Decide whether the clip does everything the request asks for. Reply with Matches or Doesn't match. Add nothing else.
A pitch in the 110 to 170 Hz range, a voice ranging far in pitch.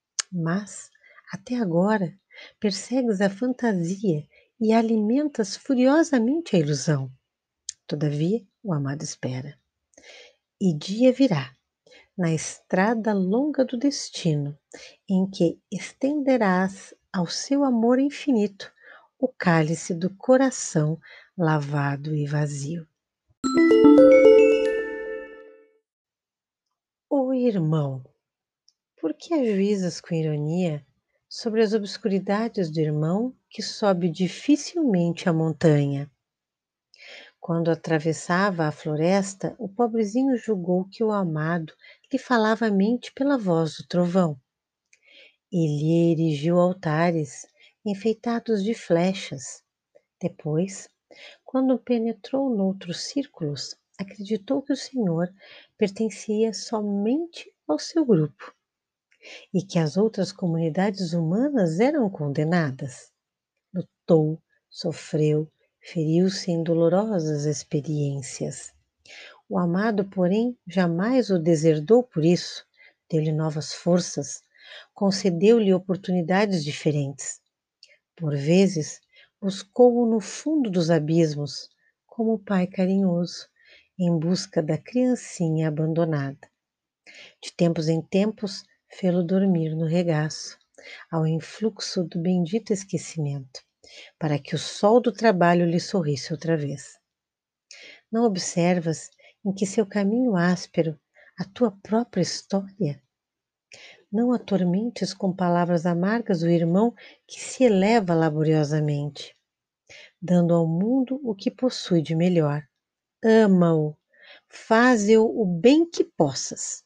Doesn't match